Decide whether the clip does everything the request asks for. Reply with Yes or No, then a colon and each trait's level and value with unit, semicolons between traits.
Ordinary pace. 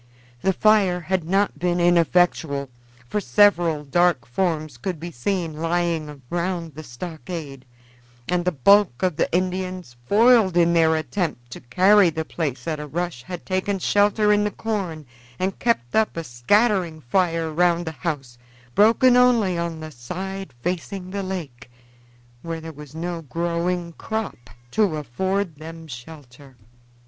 Yes: average, 150 wpm